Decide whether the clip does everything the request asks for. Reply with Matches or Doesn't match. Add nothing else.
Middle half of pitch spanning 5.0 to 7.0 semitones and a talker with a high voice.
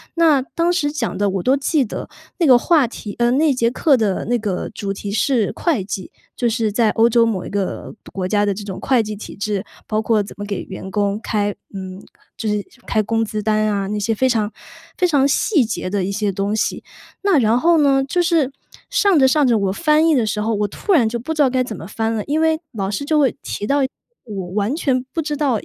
Matches